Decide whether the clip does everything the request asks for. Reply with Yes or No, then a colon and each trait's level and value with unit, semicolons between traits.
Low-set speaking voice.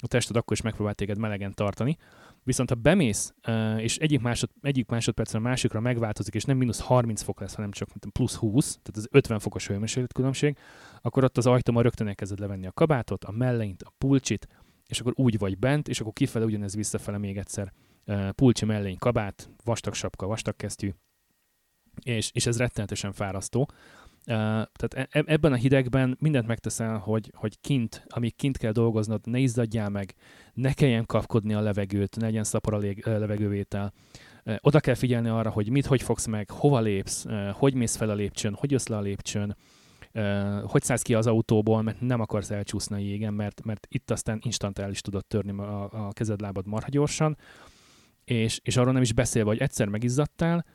Yes: low, 110 Hz